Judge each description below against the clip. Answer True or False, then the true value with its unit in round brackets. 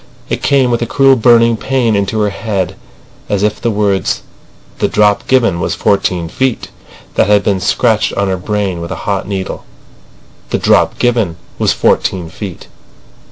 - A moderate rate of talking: True (160 wpm)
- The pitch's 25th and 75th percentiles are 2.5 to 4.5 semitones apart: True (3.4 semitones)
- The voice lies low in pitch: True (105 Hz)